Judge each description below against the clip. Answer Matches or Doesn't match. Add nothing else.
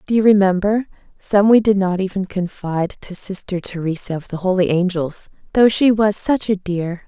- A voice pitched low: Doesn't match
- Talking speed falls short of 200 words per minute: Matches